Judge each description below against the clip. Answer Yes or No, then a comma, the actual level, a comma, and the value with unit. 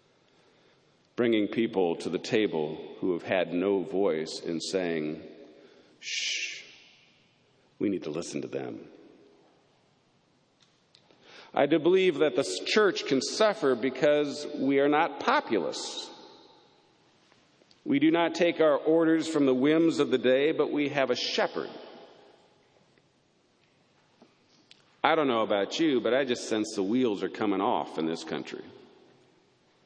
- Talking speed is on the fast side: No, slow, 135 wpm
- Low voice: No, medium, 145 Hz